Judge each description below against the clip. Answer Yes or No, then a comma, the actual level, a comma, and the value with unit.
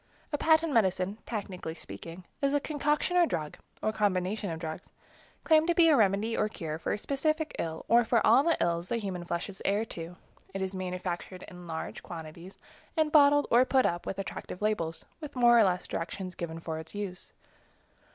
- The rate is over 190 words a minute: Yes, average, 200 wpm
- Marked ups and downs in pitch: Yes, wide, 7.0 semitones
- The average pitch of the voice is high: Yes, high, 195 Hz